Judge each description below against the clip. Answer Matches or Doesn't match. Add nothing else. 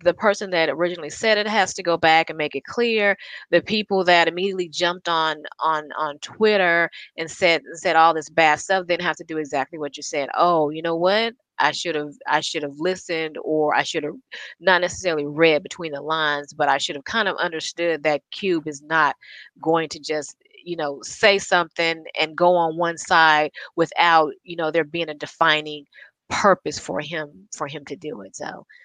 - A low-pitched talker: Doesn't match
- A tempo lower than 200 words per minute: Doesn't match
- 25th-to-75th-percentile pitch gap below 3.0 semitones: Matches